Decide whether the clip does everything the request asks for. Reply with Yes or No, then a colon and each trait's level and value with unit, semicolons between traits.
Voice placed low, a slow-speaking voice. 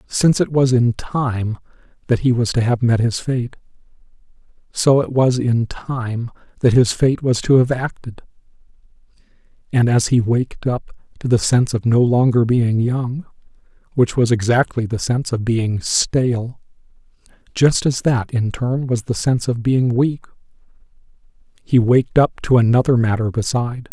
No: low, 120 Hz; average, 160 wpm